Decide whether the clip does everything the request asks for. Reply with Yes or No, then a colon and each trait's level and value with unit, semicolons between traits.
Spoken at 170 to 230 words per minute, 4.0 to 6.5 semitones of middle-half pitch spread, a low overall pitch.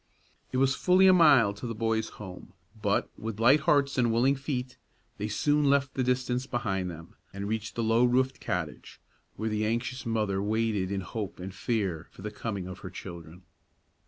Yes: average, 190 wpm; average, 4.4 semitones; low, 115 Hz